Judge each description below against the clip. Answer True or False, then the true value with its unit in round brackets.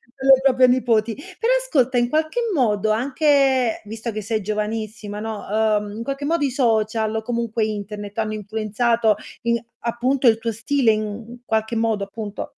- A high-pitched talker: True (225 Hz)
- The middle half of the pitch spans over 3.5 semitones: False (2.9 semitones)